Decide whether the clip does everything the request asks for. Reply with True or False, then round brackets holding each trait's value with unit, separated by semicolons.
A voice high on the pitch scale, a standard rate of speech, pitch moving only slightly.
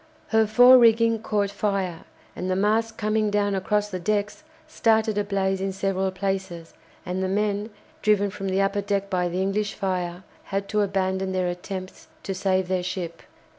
True (195 Hz; 175 wpm; 1.9 semitones)